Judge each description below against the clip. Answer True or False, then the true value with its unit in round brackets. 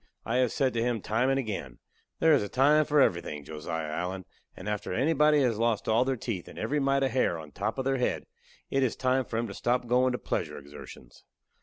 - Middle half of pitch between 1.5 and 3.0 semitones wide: False (5.4 semitones)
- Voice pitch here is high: False (120 Hz)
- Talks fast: True (240 wpm)